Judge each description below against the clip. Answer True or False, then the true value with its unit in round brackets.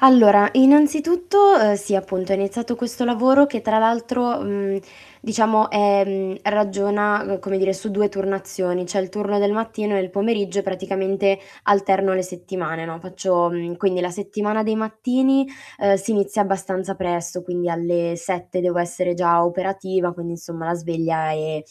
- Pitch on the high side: True (195 Hz)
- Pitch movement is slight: False (3.0 semitones)